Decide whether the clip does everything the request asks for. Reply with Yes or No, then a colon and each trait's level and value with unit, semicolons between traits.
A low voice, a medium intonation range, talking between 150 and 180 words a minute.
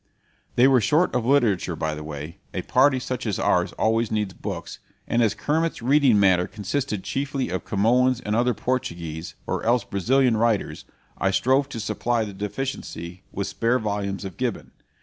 Yes: low, 115 Hz; average, 4.8 semitones; average, 170 wpm